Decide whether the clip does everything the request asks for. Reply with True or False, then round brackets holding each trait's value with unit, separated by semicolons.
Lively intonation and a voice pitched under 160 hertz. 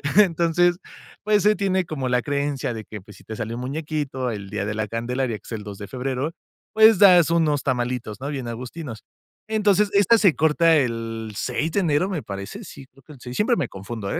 True (6.8 semitones; 135 Hz)